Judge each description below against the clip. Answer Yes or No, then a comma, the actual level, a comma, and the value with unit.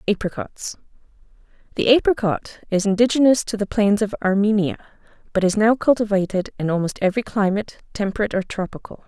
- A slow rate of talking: Yes, slow, 130 wpm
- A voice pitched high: Yes, high, 210 Hz